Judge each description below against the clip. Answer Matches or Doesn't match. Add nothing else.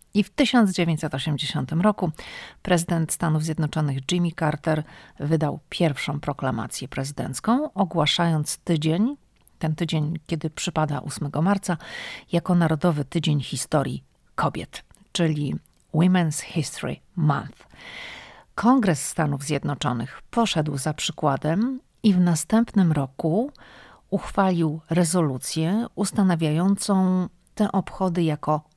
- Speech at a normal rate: Doesn't match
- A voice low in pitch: Doesn't match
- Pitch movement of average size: Matches